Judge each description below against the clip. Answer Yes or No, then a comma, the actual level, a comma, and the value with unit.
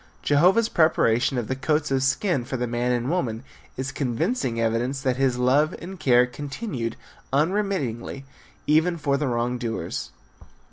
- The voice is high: No, low, 135 Hz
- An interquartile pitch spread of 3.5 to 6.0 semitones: Yes, average, 4.1 semitones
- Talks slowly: No, average, 150 wpm